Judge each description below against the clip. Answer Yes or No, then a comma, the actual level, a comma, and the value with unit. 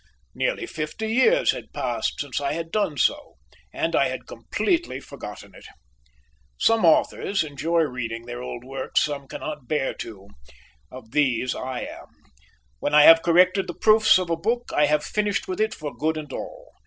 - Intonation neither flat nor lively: No, wide, 6.9 semitones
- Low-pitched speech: No, medium, 155 Hz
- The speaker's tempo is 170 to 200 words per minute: Yes, average, 175 wpm